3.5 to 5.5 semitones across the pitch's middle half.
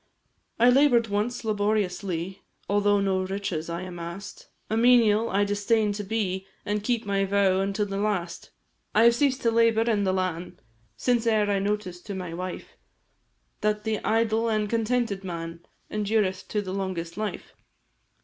No: average, 2.8 semitones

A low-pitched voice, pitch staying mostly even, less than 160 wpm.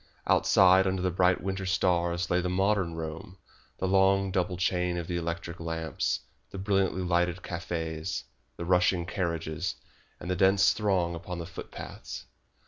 Yes: very low, 90 Hz; narrow, 1.8 semitones; average, 150 wpm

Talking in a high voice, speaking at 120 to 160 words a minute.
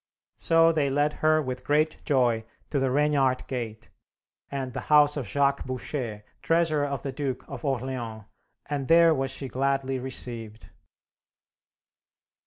No: low, 135 Hz; average, 140 wpm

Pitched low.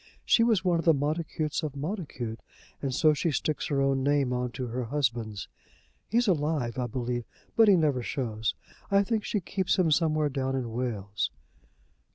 No: medium, 145 Hz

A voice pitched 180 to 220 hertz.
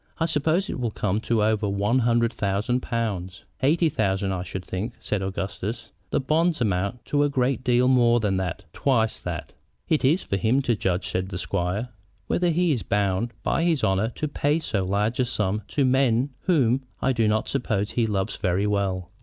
No: low, 115 Hz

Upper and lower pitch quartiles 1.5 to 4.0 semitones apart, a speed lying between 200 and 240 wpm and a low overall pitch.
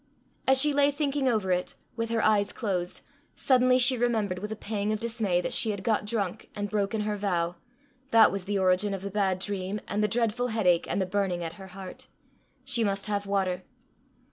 No: average, 3.1 semitones; fast, 205 wpm; high, 205 Hz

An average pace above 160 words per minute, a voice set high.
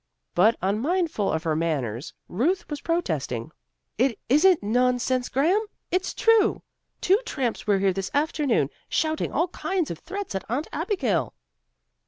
No: average, 140 wpm; very high, 255 Hz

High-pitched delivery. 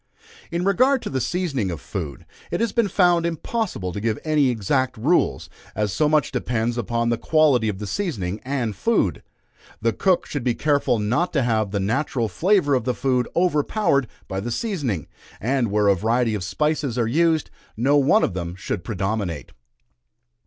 No: low, 125 Hz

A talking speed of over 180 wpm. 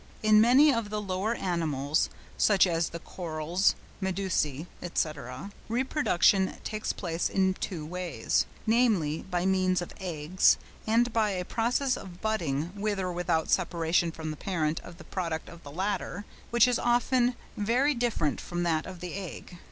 No: average, 160 wpm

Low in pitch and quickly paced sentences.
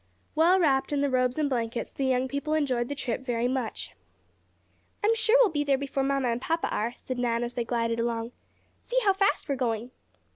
No: very high, 260 Hz; fast, 215 wpm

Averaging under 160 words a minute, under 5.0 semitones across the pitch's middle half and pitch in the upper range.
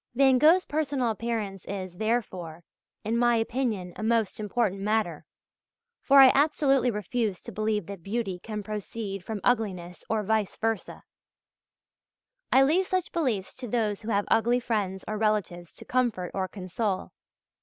Yes: average, 150 wpm; average, 3.8 semitones; high, 220 Hz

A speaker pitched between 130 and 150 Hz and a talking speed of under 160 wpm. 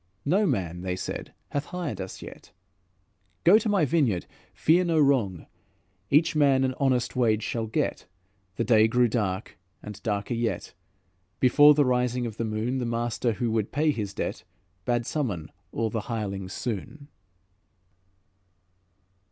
No: low, 120 Hz; average, 150 wpm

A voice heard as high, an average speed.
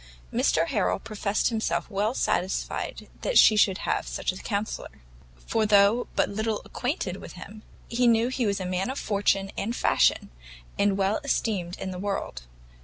Yes: high, 205 Hz; average, 170 wpm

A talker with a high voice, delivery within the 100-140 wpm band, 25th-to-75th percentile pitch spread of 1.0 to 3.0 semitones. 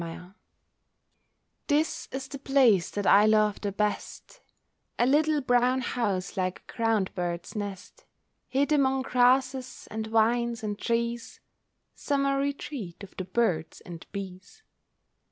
No: high, 230 Hz; slow, 135 wpm; average, 4.9 semitones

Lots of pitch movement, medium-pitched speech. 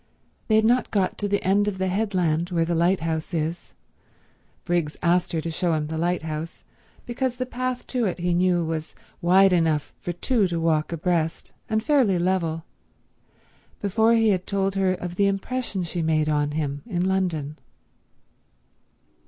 No: average, 3.5 semitones; medium, 180 Hz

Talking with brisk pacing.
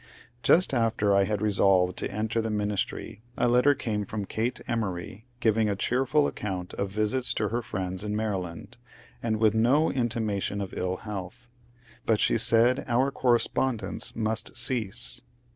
No: average, 155 wpm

